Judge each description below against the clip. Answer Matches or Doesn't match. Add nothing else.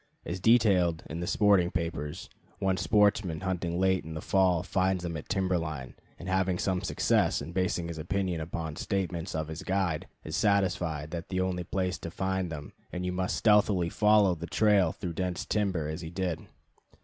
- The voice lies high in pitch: Doesn't match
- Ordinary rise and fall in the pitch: Doesn't match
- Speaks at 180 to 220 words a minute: Matches